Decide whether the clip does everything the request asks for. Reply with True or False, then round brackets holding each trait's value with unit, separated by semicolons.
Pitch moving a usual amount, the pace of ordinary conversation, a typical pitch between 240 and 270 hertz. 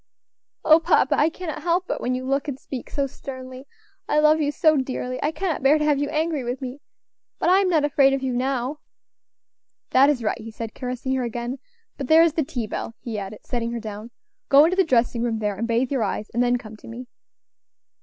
False (4.0 semitones; 230 wpm; 260 Hz)